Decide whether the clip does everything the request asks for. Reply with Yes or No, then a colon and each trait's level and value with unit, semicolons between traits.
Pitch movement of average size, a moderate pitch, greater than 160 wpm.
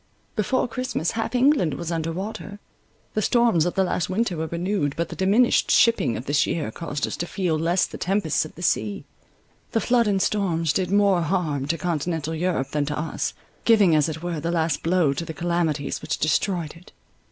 Yes: average, 4.1 semitones; medium, 170 Hz; average, 200 wpm